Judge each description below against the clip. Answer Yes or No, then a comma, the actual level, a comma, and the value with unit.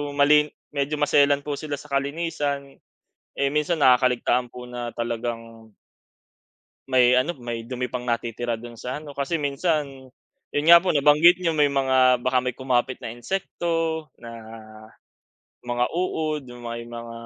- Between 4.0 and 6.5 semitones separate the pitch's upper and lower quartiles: No, average, 3.6 semitones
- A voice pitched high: No, low, 135 Hz